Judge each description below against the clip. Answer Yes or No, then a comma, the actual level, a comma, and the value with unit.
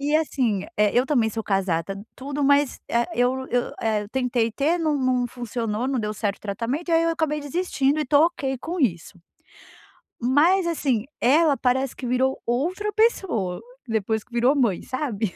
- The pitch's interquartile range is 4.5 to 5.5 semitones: Yes, average, 4.8 semitones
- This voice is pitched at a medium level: No, very high, 255 Hz